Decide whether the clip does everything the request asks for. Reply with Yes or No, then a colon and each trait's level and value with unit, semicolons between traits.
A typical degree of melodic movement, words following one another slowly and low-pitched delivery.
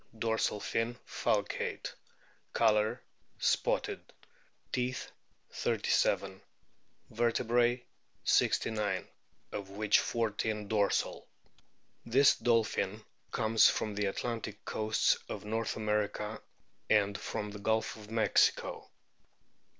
No: narrow, 1.6 semitones; slow, 90 wpm; low, 110 Hz